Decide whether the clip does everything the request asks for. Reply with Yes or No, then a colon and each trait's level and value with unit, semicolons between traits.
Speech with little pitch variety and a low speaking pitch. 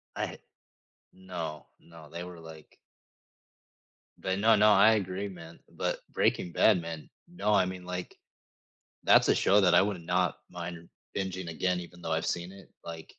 Yes: narrow, 2.3 semitones; very low, 90 Hz